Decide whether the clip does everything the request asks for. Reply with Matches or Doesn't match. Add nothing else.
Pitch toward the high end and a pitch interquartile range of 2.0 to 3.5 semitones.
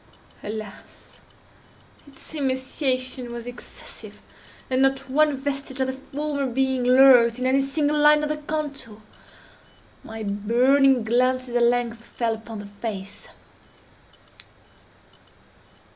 Matches